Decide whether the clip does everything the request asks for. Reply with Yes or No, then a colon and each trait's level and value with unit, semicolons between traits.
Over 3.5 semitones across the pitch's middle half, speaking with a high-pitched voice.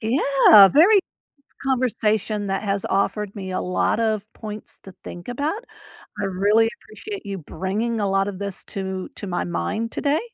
No: average, 3.0 semitones; high, 210 Hz